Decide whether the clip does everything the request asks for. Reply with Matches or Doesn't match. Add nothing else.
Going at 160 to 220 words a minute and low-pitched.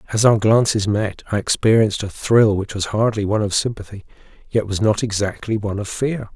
Matches